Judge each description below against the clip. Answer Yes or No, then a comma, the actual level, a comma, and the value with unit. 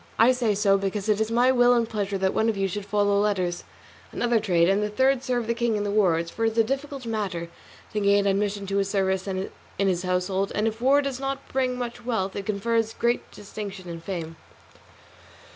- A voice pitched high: Yes, high, 210 Hz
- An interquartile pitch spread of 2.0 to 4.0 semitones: Yes, average, 3.3 semitones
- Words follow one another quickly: Yes, fast, 220 wpm